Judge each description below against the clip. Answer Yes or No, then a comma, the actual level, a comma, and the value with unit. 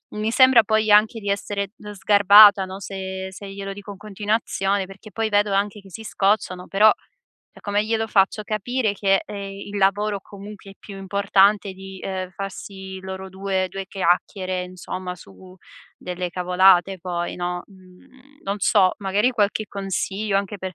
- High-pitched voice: Yes, high, 195 Hz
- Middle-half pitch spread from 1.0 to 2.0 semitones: Yes, narrow, 1.7 semitones